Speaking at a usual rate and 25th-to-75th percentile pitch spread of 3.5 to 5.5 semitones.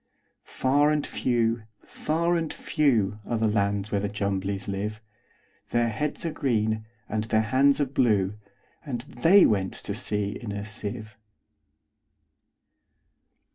No: slow, 120 wpm; average, 4.2 semitones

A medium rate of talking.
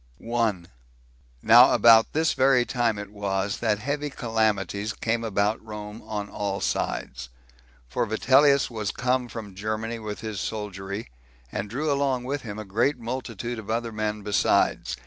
Yes: average, 150 wpm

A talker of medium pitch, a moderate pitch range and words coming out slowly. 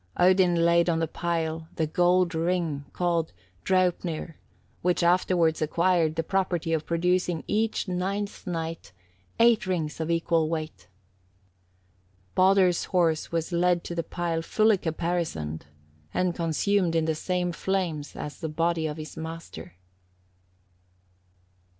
No: medium, 170 Hz; narrow, 2.0 semitones; slow, 125 wpm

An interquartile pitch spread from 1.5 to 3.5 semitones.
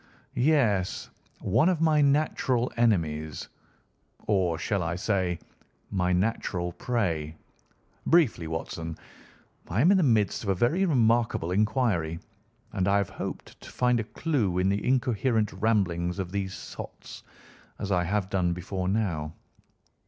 No: average, 5.2 semitones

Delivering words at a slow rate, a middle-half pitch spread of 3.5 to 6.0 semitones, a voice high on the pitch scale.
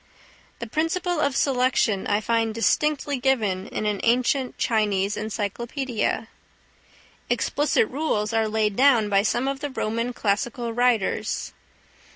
Yes: slow, 125 wpm; average, 3.9 semitones; high, 235 Hz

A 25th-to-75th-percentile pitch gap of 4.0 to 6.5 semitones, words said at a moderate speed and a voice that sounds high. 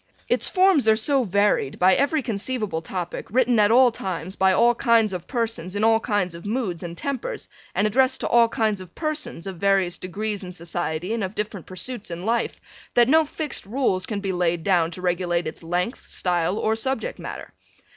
Yes: average, 4.8 semitones; average, 195 wpm; high, 205 Hz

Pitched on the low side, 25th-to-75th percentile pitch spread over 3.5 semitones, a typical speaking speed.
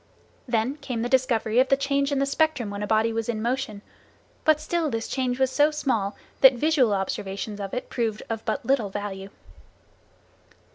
No: high, 240 Hz; average, 4.2 semitones; average, 185 wpm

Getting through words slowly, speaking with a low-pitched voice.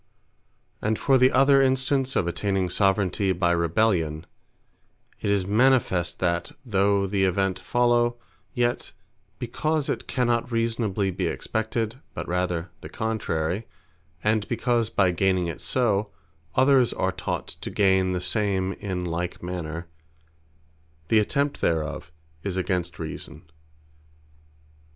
Yes: slow, 125 wpm; low, 100 Hz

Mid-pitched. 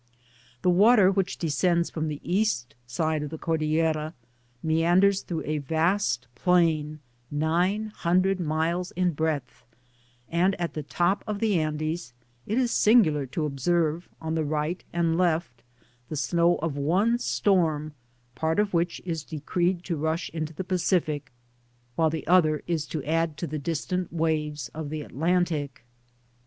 Yes: medium, 165 Hz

